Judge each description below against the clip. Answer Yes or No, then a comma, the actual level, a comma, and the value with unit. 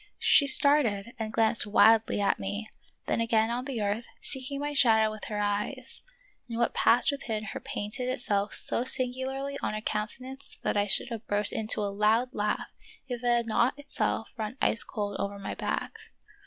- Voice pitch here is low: No, high, 225 Hz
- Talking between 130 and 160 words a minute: No, average, 185 wpm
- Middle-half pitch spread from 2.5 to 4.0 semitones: Yes, average, 3.4 semitones